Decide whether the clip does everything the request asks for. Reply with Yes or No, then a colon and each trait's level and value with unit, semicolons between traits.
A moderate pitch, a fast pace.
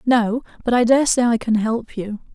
No: high, 230 Hz; fast, 230 wpm